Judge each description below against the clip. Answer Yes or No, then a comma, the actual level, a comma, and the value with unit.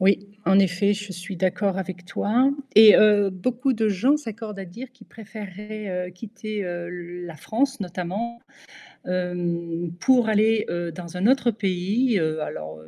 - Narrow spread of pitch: No, average, 3.6 semitones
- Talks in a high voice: Yes, high, 200 Hz